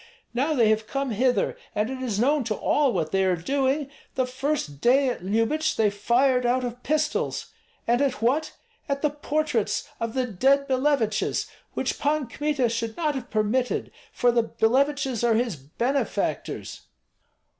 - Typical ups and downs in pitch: Yes, average, 3.7 semitones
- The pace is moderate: Yes, average, 165 wpm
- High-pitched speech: Yes, very high, 250 Hz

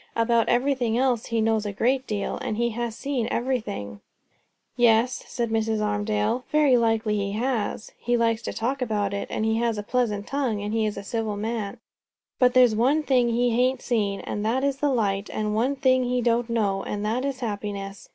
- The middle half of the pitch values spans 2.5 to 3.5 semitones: Yes, average, 2.8 semitones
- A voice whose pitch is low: No, high, 230 Hz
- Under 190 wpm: No, fast, 205 wpm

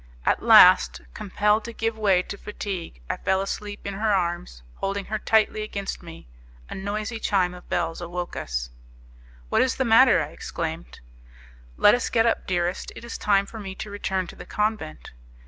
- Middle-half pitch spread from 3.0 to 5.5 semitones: Yes, average, 3.5 semitones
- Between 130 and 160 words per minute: No, average, 180 wpm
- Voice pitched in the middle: No, high, 195 Hz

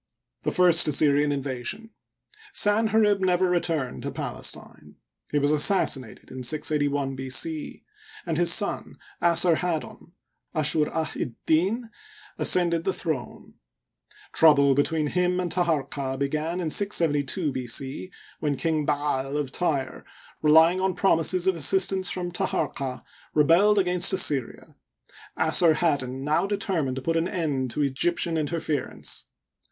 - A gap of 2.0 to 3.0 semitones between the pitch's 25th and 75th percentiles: No, average, 4.1 semitones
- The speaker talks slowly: Yes, slow, 125 wpm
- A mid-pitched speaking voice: Yes, medium, 160 Hz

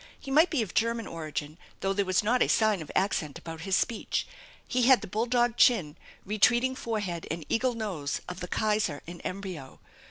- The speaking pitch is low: No, high, 205 Hz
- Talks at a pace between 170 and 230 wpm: Yes, average, 195 wpm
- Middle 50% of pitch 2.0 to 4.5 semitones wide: No, wide, 5.5 semitones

